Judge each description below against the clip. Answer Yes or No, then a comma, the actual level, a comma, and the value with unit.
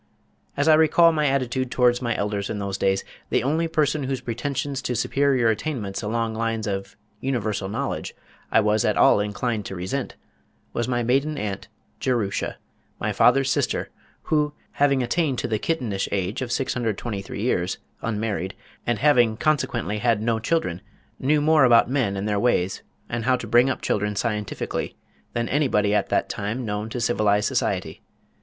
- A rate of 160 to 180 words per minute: Yes, average, 165 wpm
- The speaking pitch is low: Yes, low, 120 Hz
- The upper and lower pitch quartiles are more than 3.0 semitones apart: Yes, average, 4.5 semitones